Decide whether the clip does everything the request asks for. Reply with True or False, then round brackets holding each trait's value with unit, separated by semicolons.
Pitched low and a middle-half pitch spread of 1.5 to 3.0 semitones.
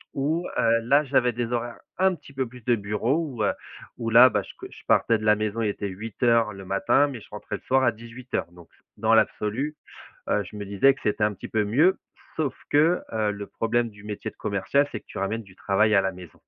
False (115 Hz; 3.7 semitones)